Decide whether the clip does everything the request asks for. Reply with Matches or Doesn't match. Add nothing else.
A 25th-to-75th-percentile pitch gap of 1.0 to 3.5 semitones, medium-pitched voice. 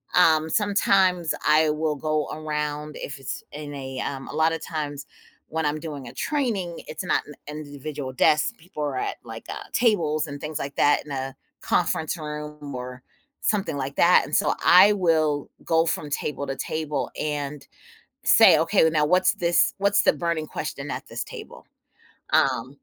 Matches